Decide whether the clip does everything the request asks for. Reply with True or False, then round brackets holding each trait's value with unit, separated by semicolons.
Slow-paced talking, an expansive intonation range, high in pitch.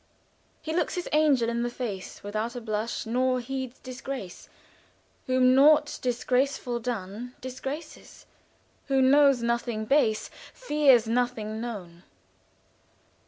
False (115 wpm; 3.0 semitones; 245 Hz)